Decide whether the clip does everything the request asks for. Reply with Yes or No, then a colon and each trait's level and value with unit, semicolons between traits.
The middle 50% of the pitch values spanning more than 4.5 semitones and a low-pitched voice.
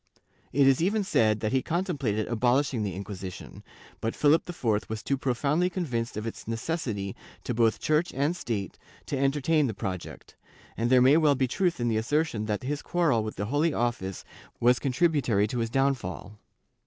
Yes: average, 5.2 semitones; low, 125 Hz